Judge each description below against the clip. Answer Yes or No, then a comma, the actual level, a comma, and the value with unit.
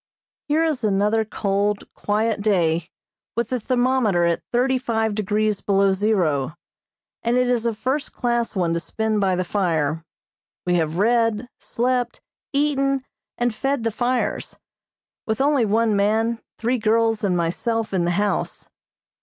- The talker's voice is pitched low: No, high, 220 Hz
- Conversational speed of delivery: Yes, average, 145 wpm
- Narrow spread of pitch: No, average, 3.6 semitones